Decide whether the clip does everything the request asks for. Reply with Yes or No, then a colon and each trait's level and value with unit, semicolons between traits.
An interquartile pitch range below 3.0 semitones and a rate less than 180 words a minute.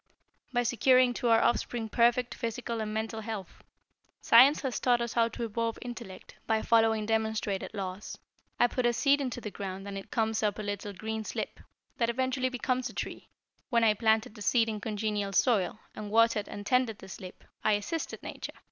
No: narrow, 2.4 semitones; average, 190 wpm